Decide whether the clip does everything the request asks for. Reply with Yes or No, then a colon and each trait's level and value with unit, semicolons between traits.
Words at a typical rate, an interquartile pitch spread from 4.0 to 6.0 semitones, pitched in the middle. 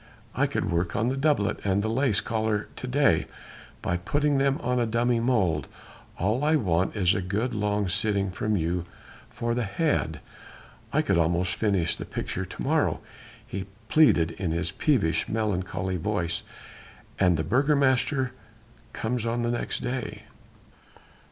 No: average, 155 wpm; wide, 5.5 semitones; low, 105 Hz